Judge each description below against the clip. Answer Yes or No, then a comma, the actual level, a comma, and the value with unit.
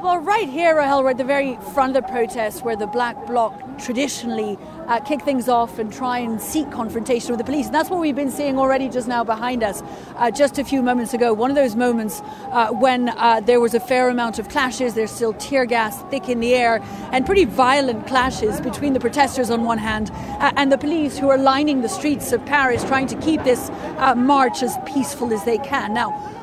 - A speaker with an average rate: No, fast, 230 wpm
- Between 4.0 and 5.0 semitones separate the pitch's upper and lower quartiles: No, average, 2.9 semitones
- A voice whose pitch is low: No, very high, 255 Hz